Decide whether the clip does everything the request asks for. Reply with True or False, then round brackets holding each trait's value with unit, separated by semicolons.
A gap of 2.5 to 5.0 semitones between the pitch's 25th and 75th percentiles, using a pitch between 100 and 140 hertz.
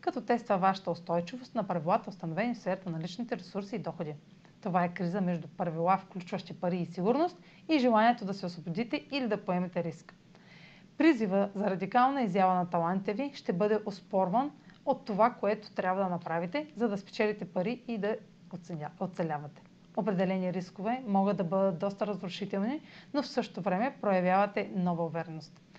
False (3.5 semitones; 195 Hz)